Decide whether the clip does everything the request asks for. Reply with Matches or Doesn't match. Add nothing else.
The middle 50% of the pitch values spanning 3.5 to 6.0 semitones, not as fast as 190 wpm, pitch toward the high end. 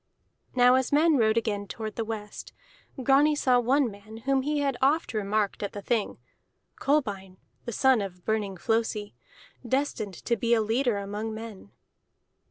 Matches